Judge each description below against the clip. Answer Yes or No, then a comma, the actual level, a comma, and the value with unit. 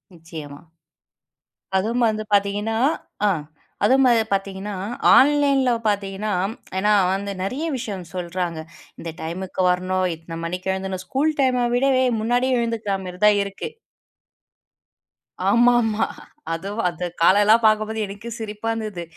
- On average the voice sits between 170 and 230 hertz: Yes, high, 205 Hz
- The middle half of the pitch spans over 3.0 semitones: Yes, average, 3.7 semitones